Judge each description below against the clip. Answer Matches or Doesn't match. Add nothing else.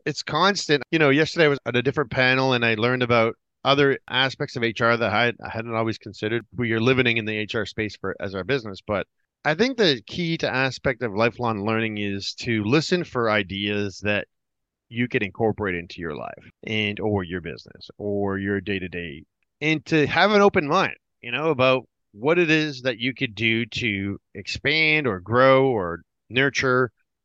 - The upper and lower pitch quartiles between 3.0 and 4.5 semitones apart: Doesn't match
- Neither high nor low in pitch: Doesn't match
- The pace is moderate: Matches